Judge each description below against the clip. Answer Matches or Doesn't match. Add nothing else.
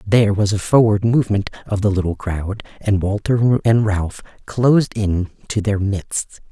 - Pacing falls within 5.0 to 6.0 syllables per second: Doesn't match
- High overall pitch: Doesn't match